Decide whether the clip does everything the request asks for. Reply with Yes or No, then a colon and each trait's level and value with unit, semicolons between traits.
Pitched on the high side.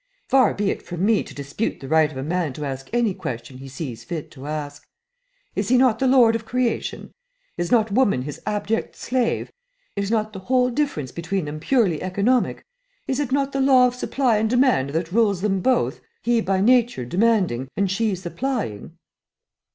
Yes: high, 205 Hz